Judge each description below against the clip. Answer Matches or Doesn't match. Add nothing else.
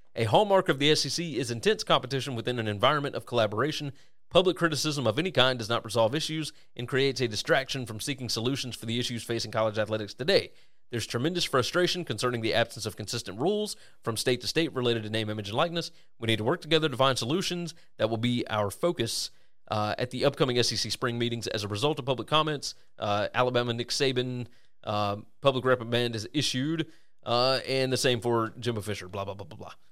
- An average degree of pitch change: Matches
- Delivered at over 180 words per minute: Matches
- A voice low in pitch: Matches